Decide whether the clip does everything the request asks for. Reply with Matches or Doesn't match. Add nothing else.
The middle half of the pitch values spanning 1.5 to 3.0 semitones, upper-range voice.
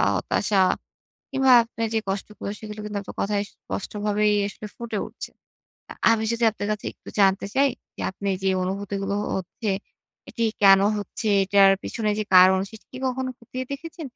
Matches